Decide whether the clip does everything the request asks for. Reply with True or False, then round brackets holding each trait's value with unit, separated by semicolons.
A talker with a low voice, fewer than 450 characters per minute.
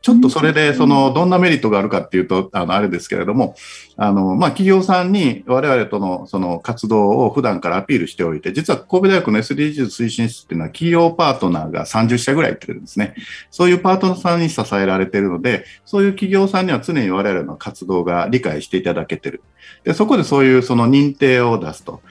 False (125 Hz; 460 characters per minute)